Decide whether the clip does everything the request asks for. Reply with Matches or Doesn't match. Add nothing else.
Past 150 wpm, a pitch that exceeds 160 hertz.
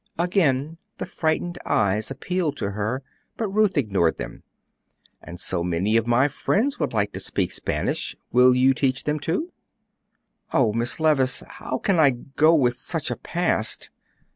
Doesn't match